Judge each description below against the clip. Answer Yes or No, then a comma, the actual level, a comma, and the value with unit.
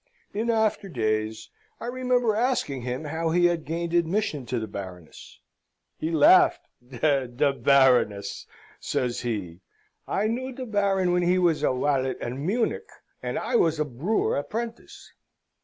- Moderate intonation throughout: No, wide, 8.7 semitones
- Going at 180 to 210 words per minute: No, average, 145 wpm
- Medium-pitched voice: Yes, medium, 160 Hz